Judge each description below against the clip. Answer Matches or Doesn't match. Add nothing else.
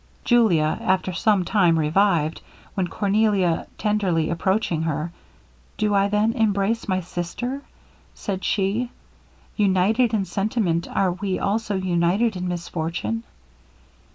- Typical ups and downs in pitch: Matches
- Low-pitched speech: Doesn't match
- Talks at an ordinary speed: Doesn't match